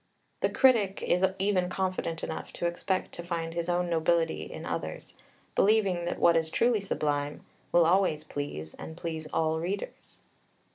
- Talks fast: No, average, 155 wpm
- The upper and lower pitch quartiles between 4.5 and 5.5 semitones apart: No, average, 2.7 semitones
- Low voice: No, medium, 170 Hz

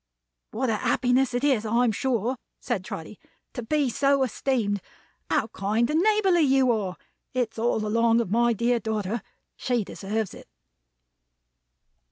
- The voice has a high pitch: Yes, high, 235 Hz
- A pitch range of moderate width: Yes, average, 3.2 semitones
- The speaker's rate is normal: Yes, average, 145 wpm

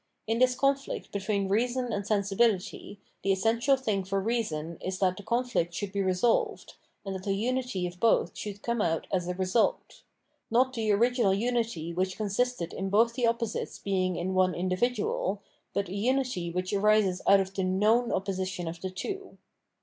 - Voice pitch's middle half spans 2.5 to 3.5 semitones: No, average, 3.9 semitones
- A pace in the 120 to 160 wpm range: No, average, 180 wpm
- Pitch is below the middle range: No, high, 200 Hz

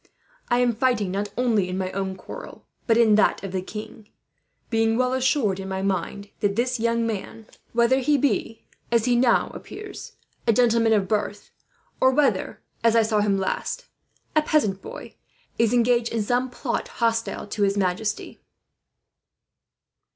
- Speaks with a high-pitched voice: Yes, high, 225 Hz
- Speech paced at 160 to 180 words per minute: Yes, average, 165 wpm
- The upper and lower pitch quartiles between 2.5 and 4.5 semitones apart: Yes, average, 3.3 semitones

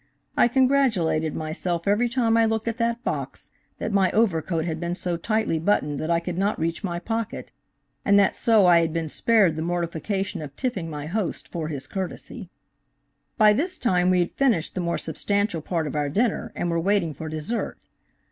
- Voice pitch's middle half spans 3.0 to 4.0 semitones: No, average, 5.1 semitones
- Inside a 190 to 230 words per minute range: Yes, average, 195 wpm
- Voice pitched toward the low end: No, medium, 180 Hz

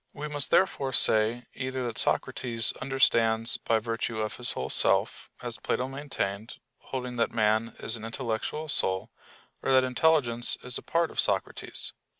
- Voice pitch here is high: No, low, 120 Hz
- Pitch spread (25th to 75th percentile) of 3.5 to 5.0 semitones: No, average, 2.9 semitones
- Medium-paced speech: Yes, average, 155 wpm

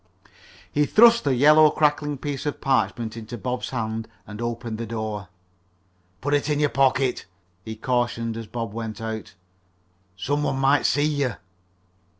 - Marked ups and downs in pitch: No, average, 4.3 semitones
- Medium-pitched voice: No, low, 125 Hz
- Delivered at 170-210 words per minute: No, average, 155 wpm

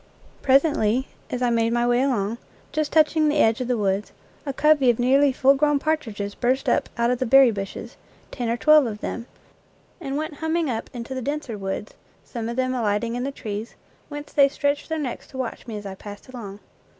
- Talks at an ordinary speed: No, fast, 210 wpm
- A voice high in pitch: Yes, very high, 250 Hz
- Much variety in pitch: No, average, 3.9 semitones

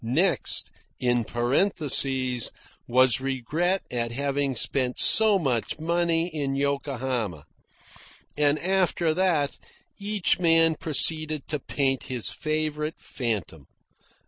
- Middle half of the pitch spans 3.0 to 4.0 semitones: No, average, 4.5 semitones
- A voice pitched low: No, medium, 145 Hz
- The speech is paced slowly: Yes, slow, 100 wpm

